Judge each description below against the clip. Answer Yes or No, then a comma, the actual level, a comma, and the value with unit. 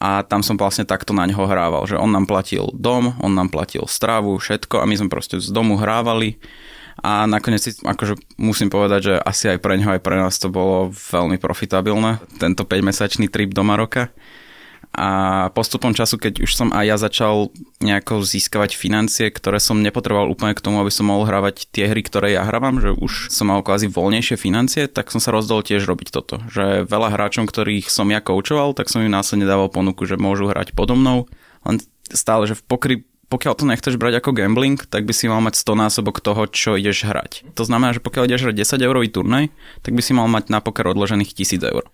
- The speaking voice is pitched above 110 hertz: No, low, 105 Hz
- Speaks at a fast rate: Yes, fast, 210 wpm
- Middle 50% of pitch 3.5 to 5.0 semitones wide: No, narrow, 2.5 semitones